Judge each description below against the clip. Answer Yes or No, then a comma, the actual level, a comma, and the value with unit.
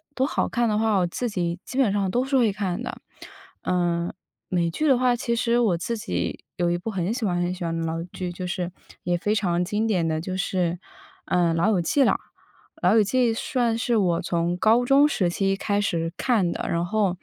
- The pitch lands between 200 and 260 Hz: No, high, 190 Hz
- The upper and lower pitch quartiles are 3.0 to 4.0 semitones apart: No, average, 4.7 semitones